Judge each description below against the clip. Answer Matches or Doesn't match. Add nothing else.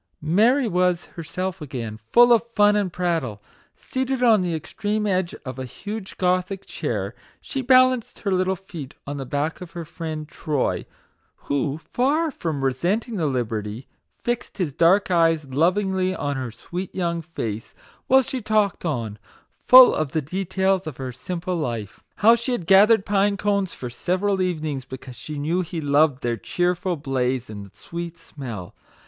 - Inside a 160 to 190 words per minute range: Matches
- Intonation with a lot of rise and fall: Matches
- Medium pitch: Matches